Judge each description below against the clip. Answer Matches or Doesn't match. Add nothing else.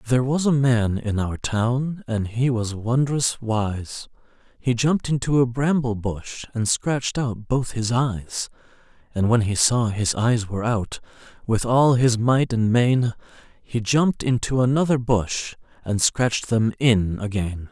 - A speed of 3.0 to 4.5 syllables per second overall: Matches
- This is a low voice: Matches